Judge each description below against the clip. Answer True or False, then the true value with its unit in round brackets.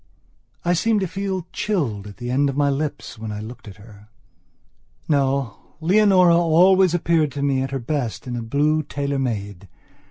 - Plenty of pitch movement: True (6.2 semitones)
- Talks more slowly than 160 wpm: False (180 wpm)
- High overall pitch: False (140 Hz)